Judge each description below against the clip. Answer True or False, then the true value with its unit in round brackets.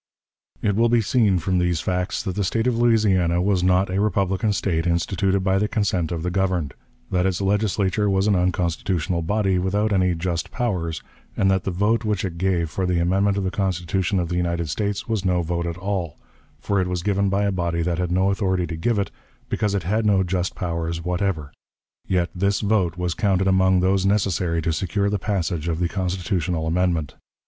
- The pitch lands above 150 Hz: False (95 Hz)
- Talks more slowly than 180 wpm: False (205 wpm)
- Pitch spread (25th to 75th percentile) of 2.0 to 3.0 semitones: True (2.4 semitones)